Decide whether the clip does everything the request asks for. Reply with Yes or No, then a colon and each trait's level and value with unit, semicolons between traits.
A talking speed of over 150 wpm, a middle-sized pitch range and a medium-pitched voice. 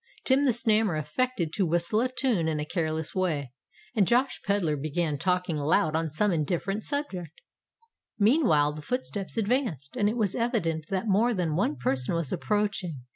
No: average, 170 wpm; wide, 6.0 semitones; medium, 180 Hz